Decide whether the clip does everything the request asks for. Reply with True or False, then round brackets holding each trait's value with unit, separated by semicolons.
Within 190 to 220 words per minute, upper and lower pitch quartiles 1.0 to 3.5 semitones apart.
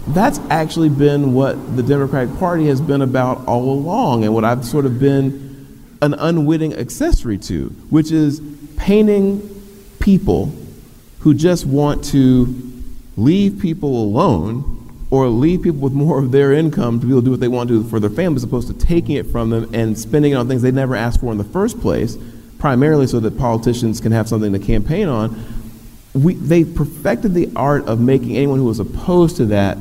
False (195 wpm; 4.5 semitones)